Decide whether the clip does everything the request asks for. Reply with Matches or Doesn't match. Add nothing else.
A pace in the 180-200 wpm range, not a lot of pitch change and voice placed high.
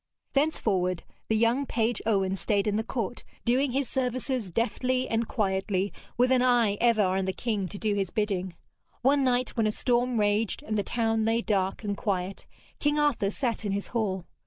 Doesn't match